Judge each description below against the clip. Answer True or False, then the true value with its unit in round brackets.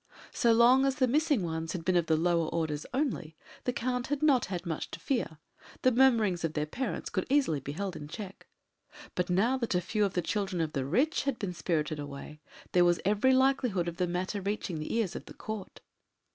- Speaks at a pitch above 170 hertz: True (185 Hz)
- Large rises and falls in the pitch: True (7.0 semitones)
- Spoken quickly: True (220 wpm)